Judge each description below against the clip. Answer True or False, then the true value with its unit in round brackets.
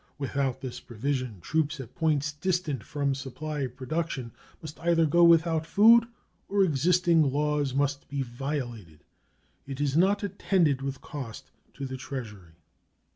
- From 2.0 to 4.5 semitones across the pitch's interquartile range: True (3.8 semitones)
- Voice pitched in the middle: True (145 Hz)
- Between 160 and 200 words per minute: False (135 wpm)